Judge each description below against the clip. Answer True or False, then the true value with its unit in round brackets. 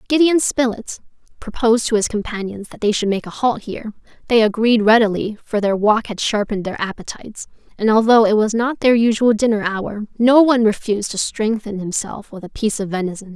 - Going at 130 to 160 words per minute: False (195 wpm)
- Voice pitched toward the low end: False (220 Hz)